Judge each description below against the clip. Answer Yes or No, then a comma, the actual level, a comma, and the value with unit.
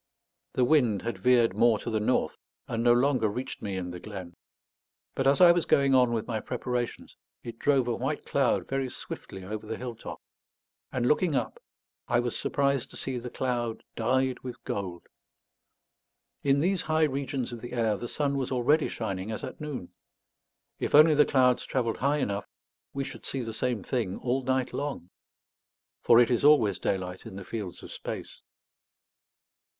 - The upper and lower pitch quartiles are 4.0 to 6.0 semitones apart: No, average, 3.5 semitones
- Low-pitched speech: Yes, low, 125 Hz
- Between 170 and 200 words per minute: Yes, average, 180 wpm